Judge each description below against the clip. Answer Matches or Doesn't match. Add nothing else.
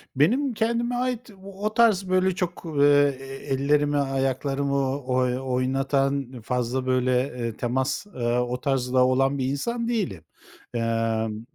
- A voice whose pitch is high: Doesn't match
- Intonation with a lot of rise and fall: Matches